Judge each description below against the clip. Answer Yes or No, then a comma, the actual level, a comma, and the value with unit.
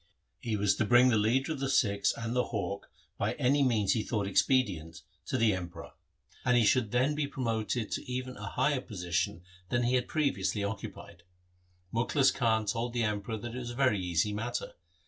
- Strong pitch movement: No, average, 3.8 semitones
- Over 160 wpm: Yes, average, 195 wpm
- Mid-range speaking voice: No, low, 115 Hz